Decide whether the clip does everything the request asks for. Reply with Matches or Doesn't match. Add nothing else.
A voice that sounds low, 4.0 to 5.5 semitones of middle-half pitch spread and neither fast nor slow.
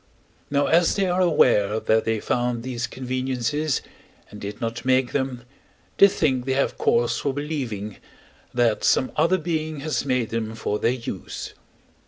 Matches